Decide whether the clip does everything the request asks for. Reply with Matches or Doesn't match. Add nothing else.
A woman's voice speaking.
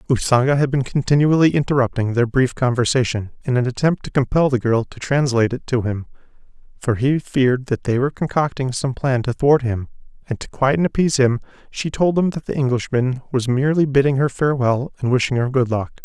Doesn't match